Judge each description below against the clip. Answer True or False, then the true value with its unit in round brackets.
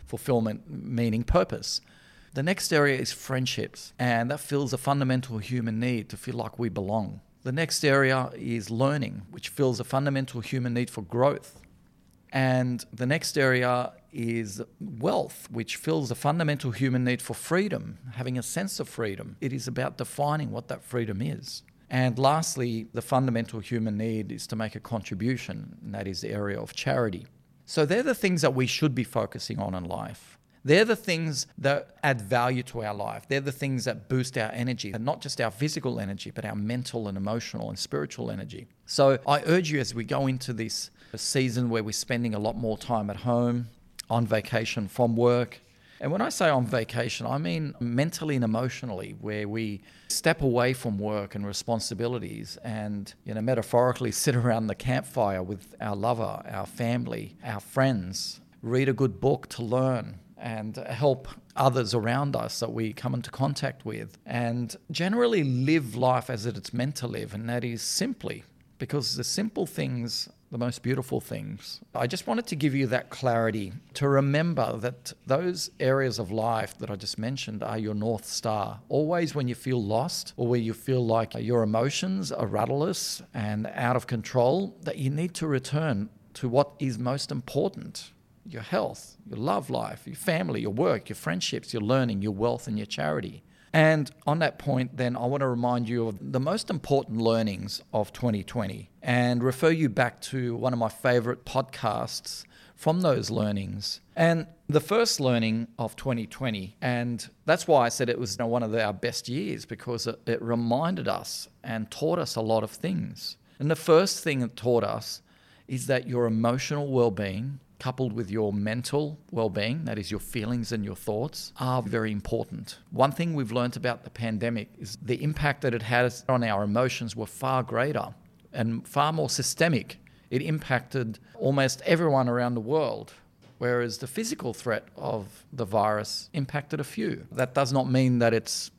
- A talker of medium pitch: False (125 Hz)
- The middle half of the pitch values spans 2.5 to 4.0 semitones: True (3.3 semitones)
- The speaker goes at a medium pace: True (180 wpm)